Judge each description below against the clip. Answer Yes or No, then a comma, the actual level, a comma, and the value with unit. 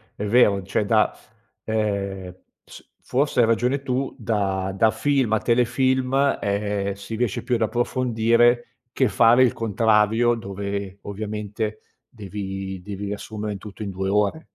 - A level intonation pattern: No, average, 3.1 semitones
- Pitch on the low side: Yes, low, 110 Hz